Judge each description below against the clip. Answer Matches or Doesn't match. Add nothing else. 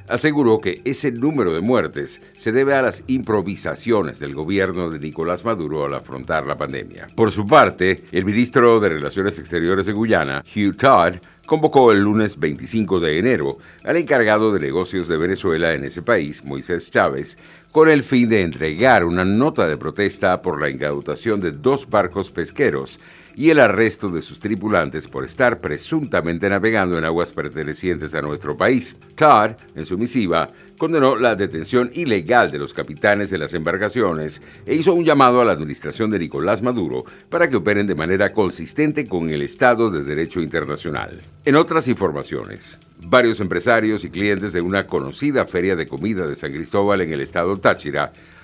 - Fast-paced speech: Doesn't match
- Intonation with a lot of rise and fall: Matches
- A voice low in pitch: Matches